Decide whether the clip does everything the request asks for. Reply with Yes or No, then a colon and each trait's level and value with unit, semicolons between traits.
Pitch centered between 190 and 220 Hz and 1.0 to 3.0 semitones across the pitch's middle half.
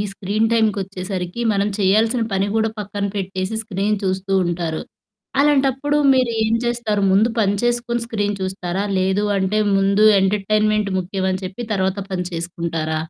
Yes: high, 200 Hz; average, 2.7 semitones